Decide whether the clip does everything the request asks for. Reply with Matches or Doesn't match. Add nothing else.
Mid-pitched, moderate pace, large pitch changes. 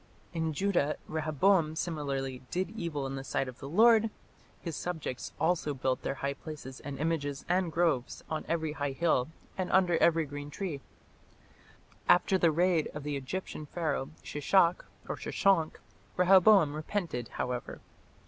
Doesn't match